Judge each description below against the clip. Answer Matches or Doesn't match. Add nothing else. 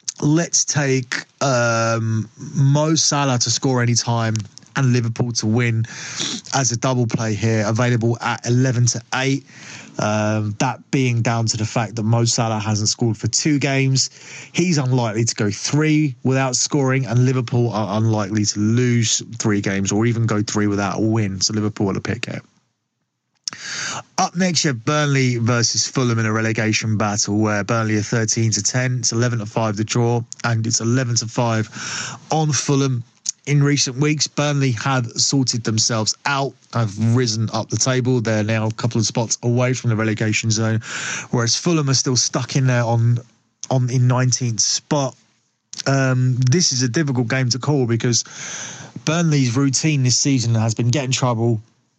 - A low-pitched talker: Matches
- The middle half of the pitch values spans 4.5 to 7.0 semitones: Doesn't match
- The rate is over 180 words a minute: Doesn't match